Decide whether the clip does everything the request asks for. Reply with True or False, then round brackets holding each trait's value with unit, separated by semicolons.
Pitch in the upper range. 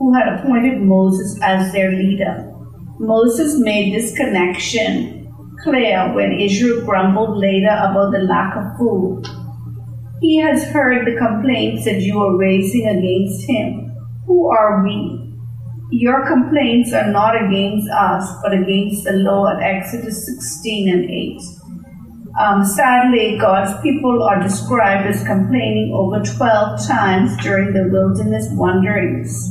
True (195 Hz)